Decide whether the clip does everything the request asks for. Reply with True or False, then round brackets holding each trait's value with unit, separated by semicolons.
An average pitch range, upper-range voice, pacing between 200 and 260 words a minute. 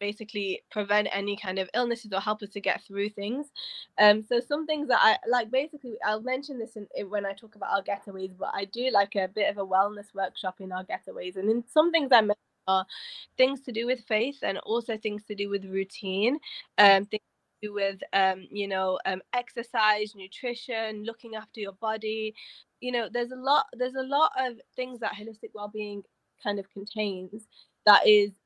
True (3.4 semitones; 210 Hz; 205 wpm)